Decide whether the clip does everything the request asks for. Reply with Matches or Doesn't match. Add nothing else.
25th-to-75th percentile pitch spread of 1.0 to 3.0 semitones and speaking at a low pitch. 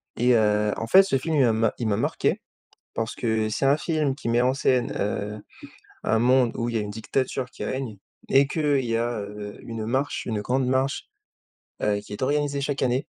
Doesn't match